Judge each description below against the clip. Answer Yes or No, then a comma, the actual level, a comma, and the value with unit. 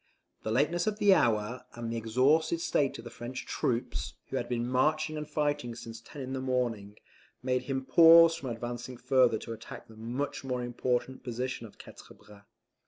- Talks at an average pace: Yes, average, 185 wpm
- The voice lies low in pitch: Yes, low, 125 Hz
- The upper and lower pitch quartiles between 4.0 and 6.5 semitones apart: No, average, 3.6 semitones